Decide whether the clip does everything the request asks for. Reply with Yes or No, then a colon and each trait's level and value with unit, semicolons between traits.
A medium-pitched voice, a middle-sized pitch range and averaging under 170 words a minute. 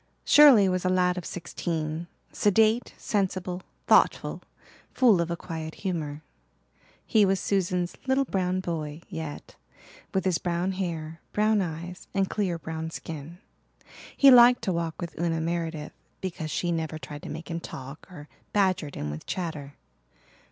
Yes: medium, 175 Hz; average, 3.0 semitones; average, 150 wpm